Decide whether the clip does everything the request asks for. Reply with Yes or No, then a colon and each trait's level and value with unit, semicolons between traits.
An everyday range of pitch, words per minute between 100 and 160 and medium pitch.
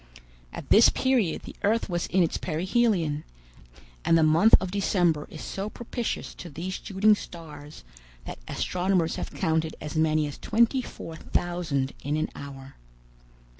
Yes: average, 4.4 semitones; average, 150 wpm; medium, 170 Hz